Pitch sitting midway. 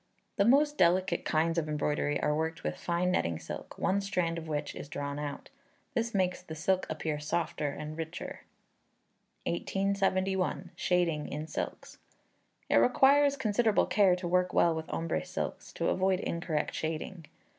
Yes: medium, 170 Hz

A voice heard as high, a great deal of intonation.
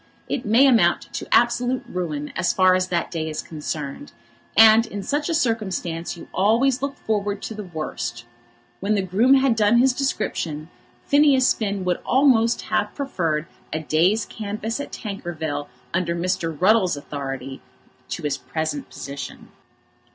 Yes: high, 200 Hz; wide, 6.4 semitones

